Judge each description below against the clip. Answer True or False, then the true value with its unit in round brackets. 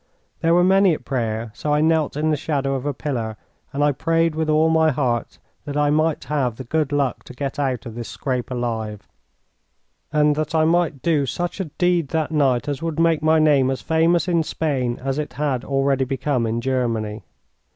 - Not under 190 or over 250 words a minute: True (205 wpm)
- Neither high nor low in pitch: True (145 Hz)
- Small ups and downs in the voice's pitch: False (3.8 semitones)